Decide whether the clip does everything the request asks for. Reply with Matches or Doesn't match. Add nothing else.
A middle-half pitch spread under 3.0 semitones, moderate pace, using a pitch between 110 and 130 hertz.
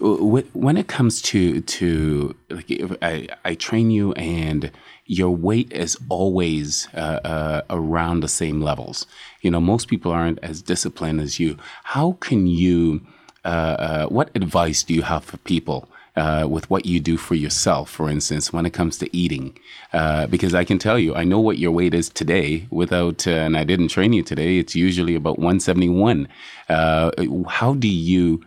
Doesn't match